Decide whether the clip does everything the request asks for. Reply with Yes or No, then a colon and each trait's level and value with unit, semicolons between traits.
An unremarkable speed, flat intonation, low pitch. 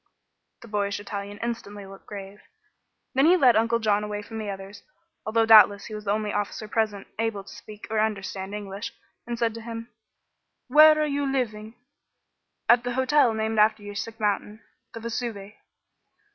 No: average, 170 wpm; narrow, 2.2 semitones; high, 215 Hz